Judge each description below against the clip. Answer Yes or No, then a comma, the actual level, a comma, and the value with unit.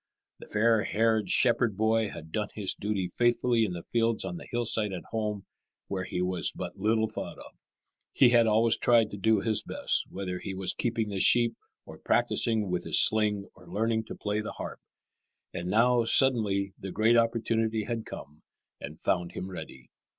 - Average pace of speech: Yes, average, 185 wpm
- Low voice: Yes, low, 110 Hz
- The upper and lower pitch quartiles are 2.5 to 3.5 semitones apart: Yes, average, 2.8 semitones